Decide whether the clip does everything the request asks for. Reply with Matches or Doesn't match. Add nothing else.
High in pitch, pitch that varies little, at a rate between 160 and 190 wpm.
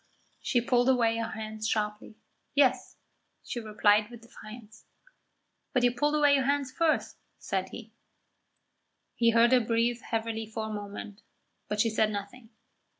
Doesn't match